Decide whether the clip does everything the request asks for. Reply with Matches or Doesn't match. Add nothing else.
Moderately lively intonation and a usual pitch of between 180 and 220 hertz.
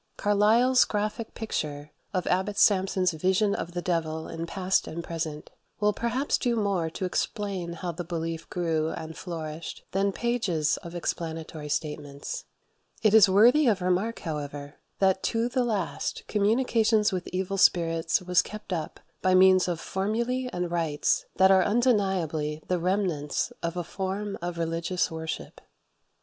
Matches